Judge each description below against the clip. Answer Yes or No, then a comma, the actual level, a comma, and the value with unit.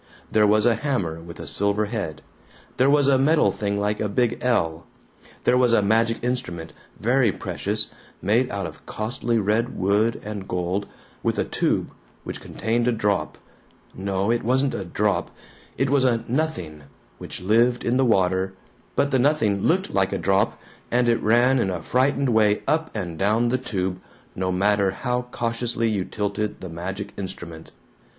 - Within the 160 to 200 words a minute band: Yes, average, 170 wpm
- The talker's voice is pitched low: Yes, low, 110 Hz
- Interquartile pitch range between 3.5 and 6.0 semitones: Yes, average, 4.2 semitones